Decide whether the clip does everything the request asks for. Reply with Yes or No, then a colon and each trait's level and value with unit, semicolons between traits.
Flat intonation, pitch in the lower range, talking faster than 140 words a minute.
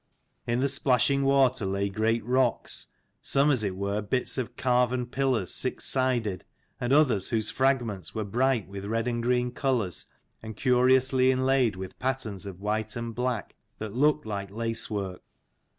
No: average, 3.7 semitones; low, 120 Hz; average, 160 wpm